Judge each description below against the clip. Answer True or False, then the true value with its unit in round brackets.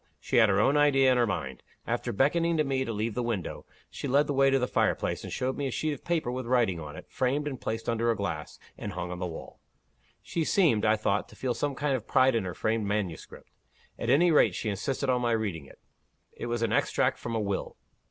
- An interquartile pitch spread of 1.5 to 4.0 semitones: False (4.6 semitones)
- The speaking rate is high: True (250 wpm)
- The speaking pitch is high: False (120 Hz)